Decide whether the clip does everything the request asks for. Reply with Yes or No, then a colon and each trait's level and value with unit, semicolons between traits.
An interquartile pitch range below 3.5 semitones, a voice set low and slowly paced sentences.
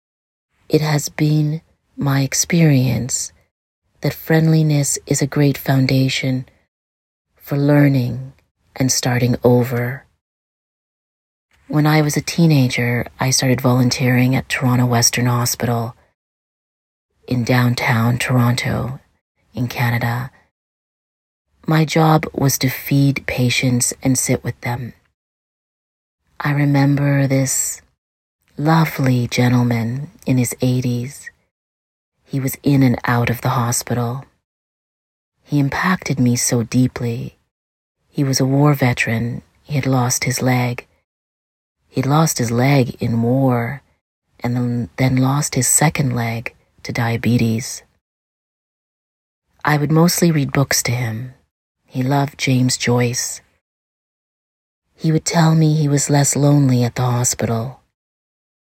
Yes: average, 2.9 semitones; low, 125 Hz; slow, 115 wpm